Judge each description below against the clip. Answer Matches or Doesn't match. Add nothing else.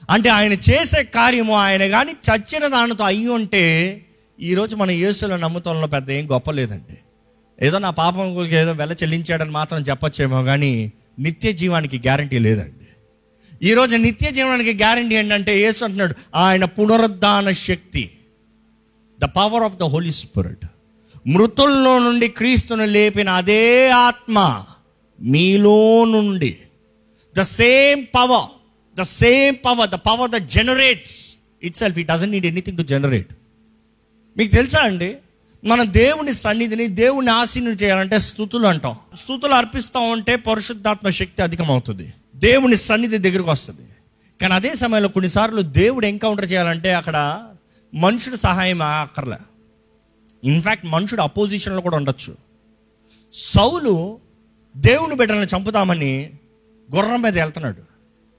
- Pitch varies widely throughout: Matches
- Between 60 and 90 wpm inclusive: Doesn't match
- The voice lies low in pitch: Doesn't match